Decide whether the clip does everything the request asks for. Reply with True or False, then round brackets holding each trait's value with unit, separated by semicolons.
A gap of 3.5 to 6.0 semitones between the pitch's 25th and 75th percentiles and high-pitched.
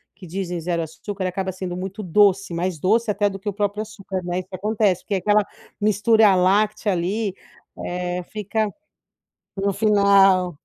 False (2.5 semitones; 195 Hz)